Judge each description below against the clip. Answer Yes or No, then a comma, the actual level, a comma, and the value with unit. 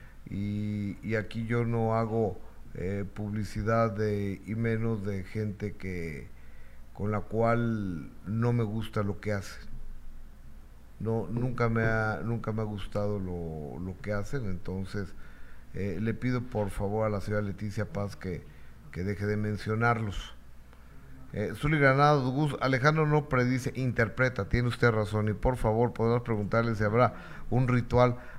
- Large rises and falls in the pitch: No, average, 3.5 semitones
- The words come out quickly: No, average, 150 wpm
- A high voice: No, low, 105 Hz